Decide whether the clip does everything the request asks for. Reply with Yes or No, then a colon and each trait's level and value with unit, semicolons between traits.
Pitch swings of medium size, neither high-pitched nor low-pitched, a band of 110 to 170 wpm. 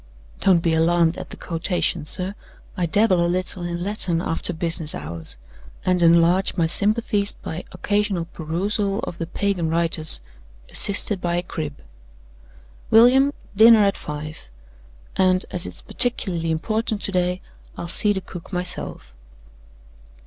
Yes: average, 3.3 semitones; medium, 180 Hz; average, 140 wpm